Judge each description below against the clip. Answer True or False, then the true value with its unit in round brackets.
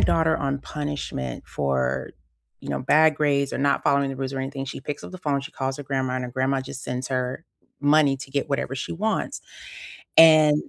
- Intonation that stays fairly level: True (2.1 semitones)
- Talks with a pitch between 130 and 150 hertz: True (140 Hz)